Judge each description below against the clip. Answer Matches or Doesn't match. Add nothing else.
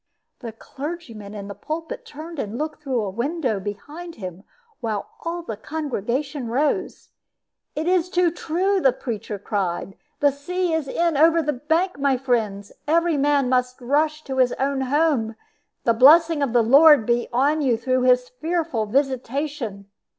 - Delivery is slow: Doesn't match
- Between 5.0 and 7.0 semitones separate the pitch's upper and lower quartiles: Matches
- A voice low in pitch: Doesn't match